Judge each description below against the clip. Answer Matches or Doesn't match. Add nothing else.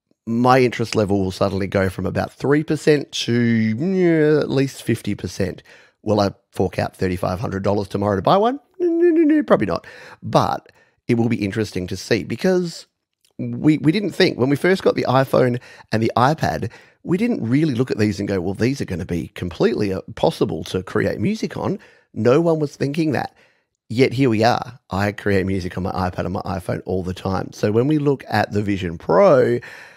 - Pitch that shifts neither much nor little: Doesn't match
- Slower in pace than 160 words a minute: Doesn't match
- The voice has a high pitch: Doesn't match